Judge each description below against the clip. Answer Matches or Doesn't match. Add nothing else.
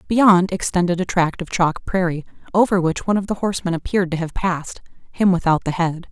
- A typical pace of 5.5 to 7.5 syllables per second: Matches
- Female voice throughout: Matches